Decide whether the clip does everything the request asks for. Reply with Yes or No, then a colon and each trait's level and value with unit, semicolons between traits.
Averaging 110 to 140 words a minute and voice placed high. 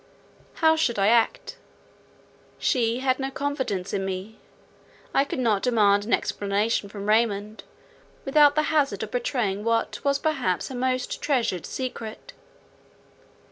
Yes: slow, 135 wpm; high, 235 Hz